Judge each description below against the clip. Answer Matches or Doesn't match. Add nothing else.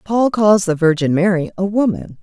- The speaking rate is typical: Matches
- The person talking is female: Matches